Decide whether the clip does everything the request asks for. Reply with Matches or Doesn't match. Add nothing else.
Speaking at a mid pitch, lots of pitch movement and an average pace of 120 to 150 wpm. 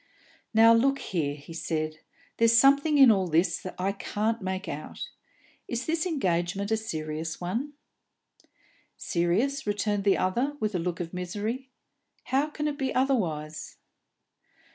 Doesn't match